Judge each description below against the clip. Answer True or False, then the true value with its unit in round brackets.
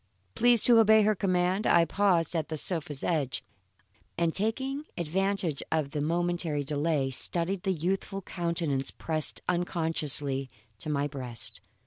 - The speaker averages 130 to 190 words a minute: True (135 wpm)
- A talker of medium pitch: True (170 Hz)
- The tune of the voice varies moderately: True (4.4 semitones)